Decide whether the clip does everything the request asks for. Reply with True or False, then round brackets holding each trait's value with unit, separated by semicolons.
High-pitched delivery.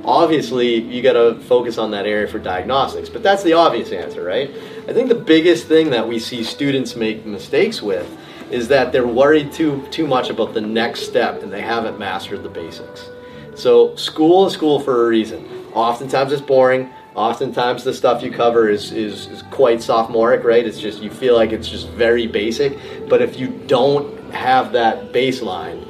False (130 Hz)